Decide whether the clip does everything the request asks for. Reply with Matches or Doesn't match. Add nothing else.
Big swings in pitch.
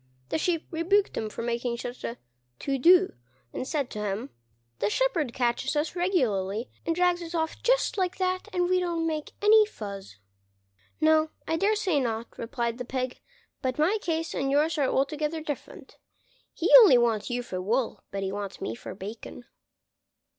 Matches